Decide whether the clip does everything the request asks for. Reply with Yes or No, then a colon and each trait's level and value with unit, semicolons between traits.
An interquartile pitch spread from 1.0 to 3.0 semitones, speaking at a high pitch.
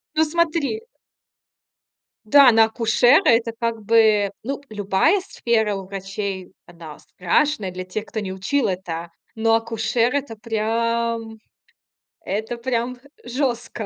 No: average, 3.4 semitones; high, 225 Hz